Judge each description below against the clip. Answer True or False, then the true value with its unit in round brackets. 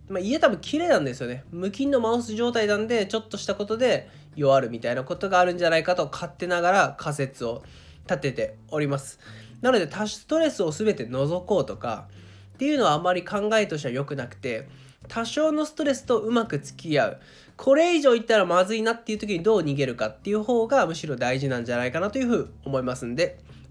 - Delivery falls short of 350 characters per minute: False (440 characters per minute)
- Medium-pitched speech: True (180 Hz)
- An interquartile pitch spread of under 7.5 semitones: False (8.8 semitones)